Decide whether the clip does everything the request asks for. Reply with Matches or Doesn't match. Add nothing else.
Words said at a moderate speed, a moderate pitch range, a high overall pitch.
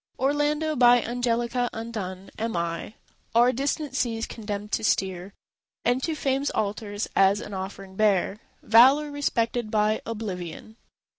Doesn't match